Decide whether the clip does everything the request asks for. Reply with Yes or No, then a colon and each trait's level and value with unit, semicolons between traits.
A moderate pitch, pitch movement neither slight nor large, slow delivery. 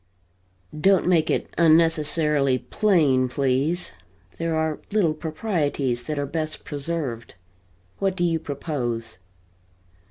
Yes: medium, 155 Hz; average, 3.3 semitones; slow, 105 wpm